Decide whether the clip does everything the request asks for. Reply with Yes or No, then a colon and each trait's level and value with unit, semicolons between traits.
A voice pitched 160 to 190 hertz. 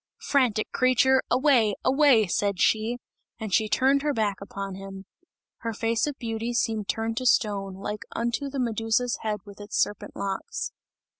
No: high, 225 Hz